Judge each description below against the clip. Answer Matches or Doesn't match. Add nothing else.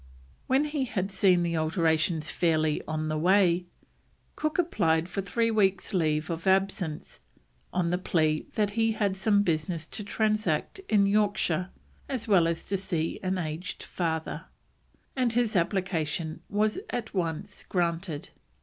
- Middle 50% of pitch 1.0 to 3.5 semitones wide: Doesn't match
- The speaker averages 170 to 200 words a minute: Doesn't match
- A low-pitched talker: Doesn't match